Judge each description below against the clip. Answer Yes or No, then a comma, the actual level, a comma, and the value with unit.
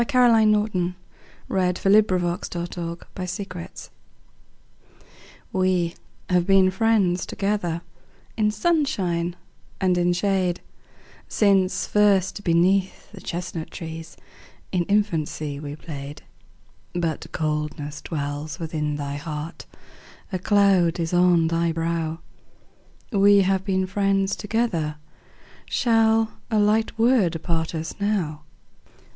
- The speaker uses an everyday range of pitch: Yes, average, 3.6 semitones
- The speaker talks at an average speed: No, slow, 105 wpm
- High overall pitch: No, medium, 180 Hz